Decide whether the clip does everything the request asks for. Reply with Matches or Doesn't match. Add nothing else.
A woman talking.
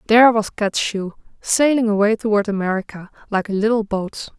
Matches